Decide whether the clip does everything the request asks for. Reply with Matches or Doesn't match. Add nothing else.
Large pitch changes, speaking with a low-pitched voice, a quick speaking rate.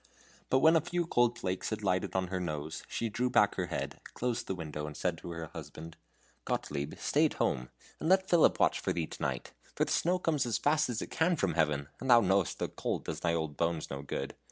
Matches